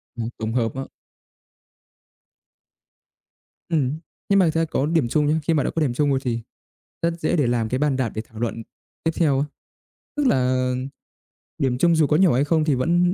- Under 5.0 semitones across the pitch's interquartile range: Yes, average, 4.5 semitones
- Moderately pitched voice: Yes, medium, 145 Hz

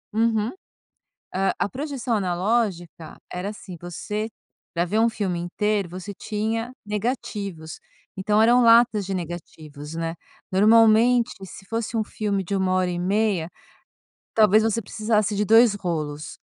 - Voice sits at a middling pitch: No, high, 205 Hz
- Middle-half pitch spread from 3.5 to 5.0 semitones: Yes, average, 3.8 semitones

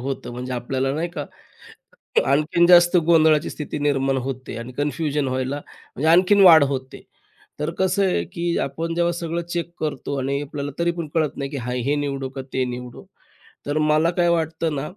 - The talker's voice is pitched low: No, medium, 150 Hz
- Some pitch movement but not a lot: Yes, average, 3.8 semitones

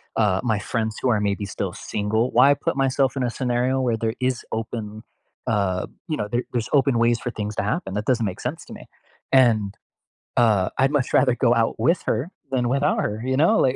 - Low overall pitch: Yes, low, 120 Hz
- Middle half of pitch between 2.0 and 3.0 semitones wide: No, average, 3.5 semitones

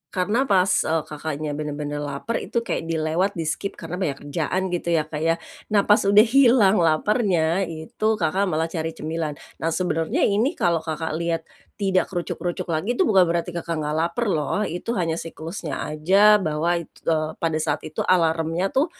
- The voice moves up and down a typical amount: Yes, average, 3.2 semitones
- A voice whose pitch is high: No, medium, 165 Hz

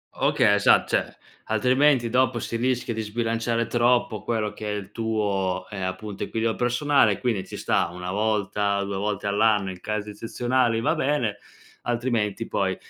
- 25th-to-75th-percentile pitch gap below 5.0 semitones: Yes, average, 2.7 semitones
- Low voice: Yes, low, 110 Hz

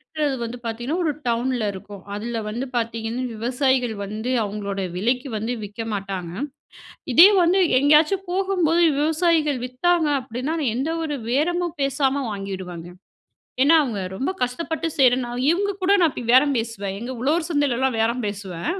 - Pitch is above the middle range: Yes, very high, 255 Hz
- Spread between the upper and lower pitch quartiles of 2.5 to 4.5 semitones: No, wide, 5.5 semitones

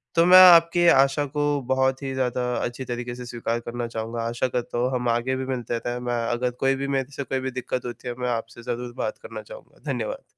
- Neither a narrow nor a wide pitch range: No, narrow, 2.1 semitones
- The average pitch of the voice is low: Yes, low, 125 Hz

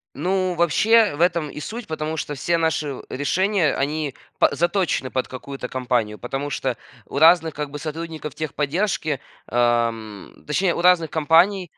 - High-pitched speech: No, medium, 155 Hz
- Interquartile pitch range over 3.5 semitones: Yes, average, 4.0 semitones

